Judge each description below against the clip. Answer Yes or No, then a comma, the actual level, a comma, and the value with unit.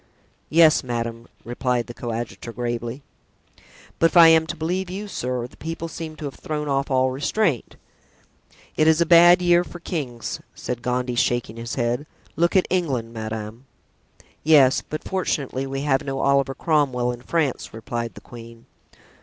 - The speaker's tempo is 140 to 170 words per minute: Yes, average, 160 wpm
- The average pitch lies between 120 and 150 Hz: Yes, low, 135 Hz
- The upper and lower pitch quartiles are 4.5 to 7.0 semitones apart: Yes, average, 5.1 semitones